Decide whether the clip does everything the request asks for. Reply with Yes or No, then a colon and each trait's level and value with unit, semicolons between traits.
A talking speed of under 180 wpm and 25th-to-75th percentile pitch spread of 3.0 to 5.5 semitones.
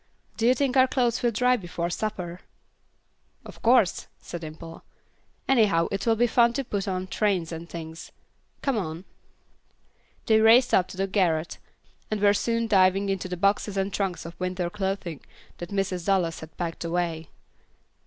Yes: average, 165 wpm; average, 4.3 semitones